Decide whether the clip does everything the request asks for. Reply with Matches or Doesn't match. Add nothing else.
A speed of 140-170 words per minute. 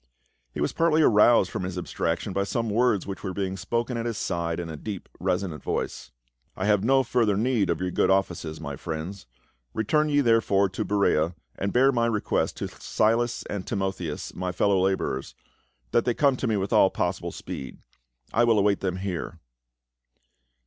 Doesn't match